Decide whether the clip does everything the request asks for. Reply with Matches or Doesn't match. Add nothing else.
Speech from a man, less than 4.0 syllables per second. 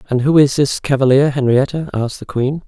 Doesn't match